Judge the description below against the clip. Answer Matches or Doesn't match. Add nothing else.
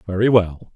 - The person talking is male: Matches